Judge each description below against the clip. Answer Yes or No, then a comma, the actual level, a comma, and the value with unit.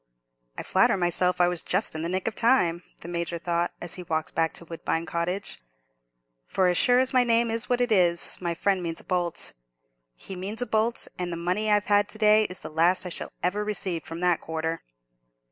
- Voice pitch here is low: No, medium, 180 Hz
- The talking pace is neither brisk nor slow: No, fast, 215 wpm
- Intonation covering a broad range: No, average, 3.7 semitones